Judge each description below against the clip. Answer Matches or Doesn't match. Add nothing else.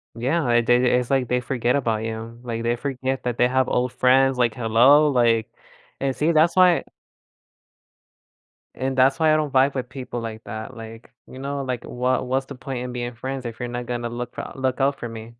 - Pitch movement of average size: Doesn't match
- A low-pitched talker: Matches